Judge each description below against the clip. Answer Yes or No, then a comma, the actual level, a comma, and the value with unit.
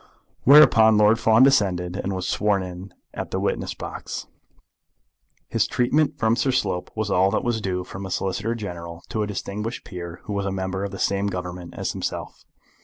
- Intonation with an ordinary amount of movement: Yes, average, 3.2 semitones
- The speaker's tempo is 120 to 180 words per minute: No, average, 190 wpm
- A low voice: Yes, low, 100 Hz